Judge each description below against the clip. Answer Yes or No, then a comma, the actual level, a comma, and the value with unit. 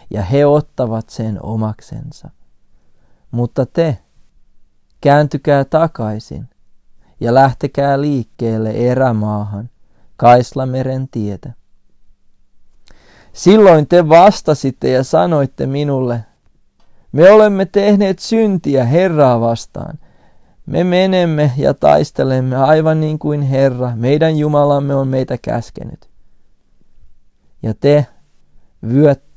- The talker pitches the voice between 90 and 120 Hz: No, low, 130 Hz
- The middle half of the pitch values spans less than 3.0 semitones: No, average, 5.2 semitones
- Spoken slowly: Yes, slow, 90 wpm